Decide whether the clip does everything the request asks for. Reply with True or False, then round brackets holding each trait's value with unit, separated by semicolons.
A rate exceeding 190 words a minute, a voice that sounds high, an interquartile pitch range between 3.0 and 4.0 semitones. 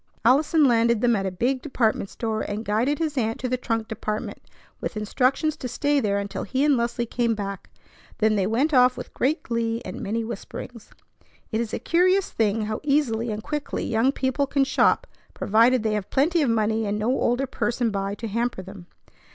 True (200 wpm; 230 Hz; 3.6 semitones)